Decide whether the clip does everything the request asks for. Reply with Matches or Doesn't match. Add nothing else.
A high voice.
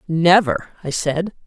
Doesn't match